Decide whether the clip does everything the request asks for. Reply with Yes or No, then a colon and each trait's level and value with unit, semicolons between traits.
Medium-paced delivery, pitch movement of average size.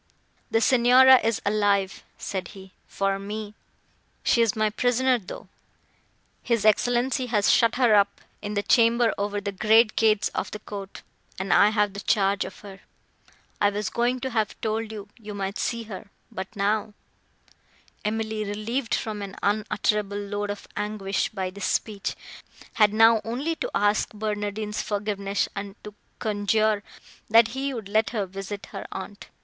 No: average, 155 wpm; narrow, 1.9 semitones